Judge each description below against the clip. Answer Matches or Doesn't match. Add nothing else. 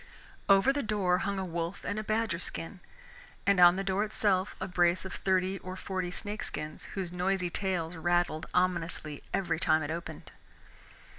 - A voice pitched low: Doesn't match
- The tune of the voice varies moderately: Doesn't match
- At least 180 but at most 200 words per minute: Doesn't match